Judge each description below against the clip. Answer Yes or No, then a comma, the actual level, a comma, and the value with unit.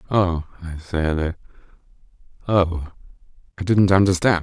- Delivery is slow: Yes, slow, 95 wpm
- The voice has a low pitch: Yes, very low, 90 Hz